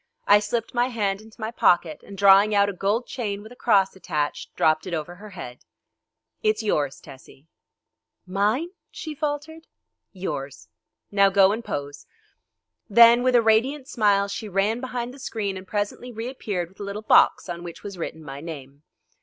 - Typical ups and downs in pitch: Yes, average, 4.5 semitones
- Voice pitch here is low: No, high, 200 Hz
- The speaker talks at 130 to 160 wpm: No, average, 175 wpm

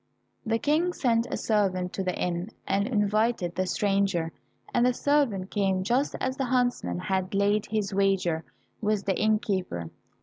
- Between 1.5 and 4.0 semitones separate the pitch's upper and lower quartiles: Yes, average, 3.7 semitones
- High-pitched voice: Yes, high, 200 Hz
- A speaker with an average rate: Yes, average, 160 wpm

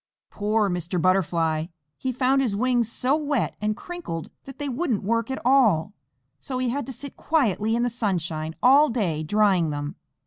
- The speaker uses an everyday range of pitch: No, wide, 6.7 semitones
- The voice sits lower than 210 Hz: No, high, 225 Hz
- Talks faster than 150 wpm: Yes, average, 175 wpm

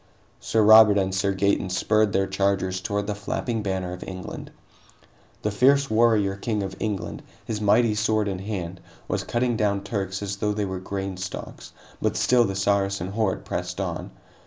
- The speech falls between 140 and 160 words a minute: No, average, 175 wpm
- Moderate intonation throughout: No, narrow, 1.9 semitones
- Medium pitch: No, low, 100 Hz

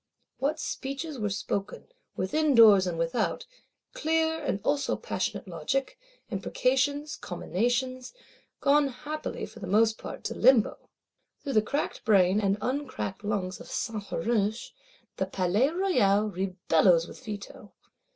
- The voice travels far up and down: Yes, wide, 6.0 semitones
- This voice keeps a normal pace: No, slow, 125 wpm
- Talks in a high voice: Yes, high, 220 Hz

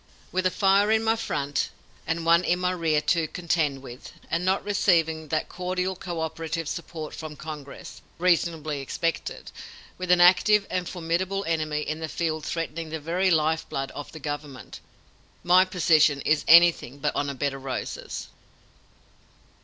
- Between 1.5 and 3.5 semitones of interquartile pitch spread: Yes, average, 2.9 semitones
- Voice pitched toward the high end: No, medium, 165 Hz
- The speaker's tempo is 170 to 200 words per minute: No, average, 160 wpm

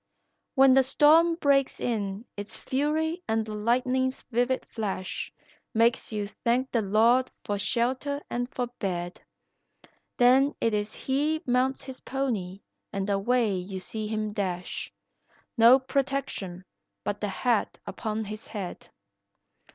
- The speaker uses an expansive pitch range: No, average, 4.3 semitones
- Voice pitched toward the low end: No, high, 235 Hz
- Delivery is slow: Yes, slow, 130 wpm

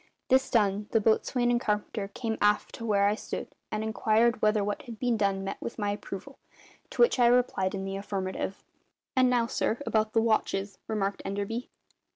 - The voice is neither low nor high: No, high, 215 Hz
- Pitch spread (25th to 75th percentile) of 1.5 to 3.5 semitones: Yes, average, 2.8 semitones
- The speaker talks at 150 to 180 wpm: No, average, 190 wpm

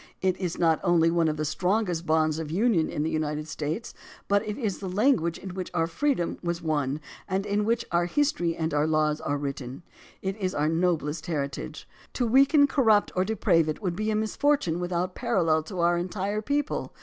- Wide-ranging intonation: No, average, 4.8 semitones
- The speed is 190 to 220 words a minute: Yes, average, 200 wpm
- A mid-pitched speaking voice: Yes, medium, 175 Hz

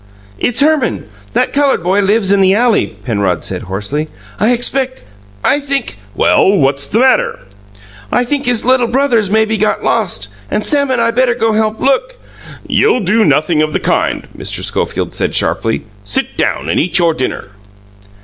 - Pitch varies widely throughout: Yes, wide, 8.5 semitones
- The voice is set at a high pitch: Yes, high, 220 Hz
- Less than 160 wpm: No, average, 180 wpm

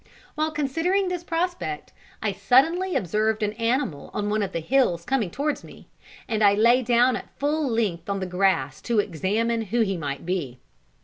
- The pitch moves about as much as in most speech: No, wide, 6.3 semitones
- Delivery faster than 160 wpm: Yes, average, 180 wpm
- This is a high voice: Yes, high, 220 Hz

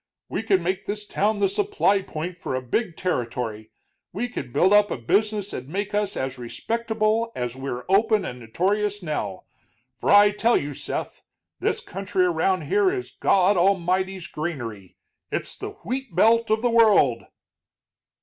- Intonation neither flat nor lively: No, wide, 6.6 semitones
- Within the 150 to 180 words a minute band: Yes, average, 160 wpm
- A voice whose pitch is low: No, high, 190 Hz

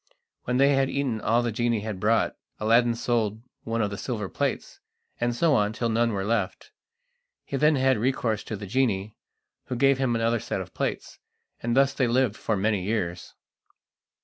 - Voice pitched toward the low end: Yes, low, 115 Hz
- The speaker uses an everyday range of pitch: Yes, average, 3.0 semitones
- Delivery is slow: No, average, 185 wpm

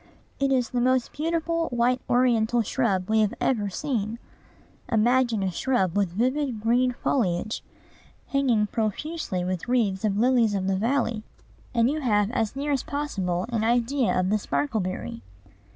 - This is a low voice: No, high, 235 Hz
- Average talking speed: Yes, average, 150 wpm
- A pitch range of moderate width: Yes, average, 4.1 semitones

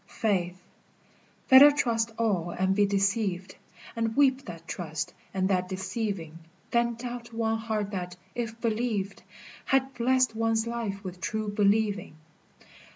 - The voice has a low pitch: No, high, 215 Hz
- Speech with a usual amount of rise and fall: Yes, average, 3.6 semitones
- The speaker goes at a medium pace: No, slow, 130 wpm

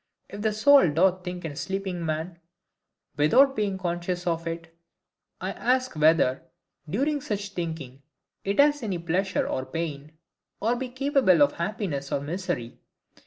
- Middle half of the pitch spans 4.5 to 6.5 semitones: Yes, average, 4.8 semitones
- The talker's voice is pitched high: No, medium, 180 Hz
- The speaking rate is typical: Yes, average, 150 wpm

